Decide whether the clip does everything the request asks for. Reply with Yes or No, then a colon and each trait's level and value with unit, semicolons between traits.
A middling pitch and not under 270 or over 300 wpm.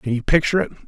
Yes: medium, 145 Hz; fast, 275 wpm